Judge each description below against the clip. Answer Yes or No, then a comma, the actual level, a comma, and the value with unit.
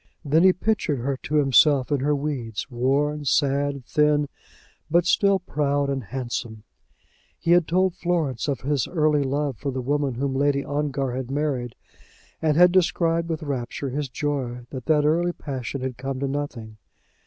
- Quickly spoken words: No, average, 165 wpm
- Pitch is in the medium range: Yes, medium, 145 Hz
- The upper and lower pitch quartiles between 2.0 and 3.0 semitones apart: Yes, narrow, 2.5 semitones